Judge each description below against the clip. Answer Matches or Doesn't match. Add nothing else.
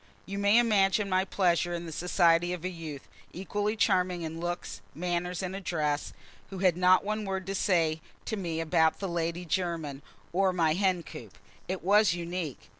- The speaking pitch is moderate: Matches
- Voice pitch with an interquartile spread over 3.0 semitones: Doesn't match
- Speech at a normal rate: Matches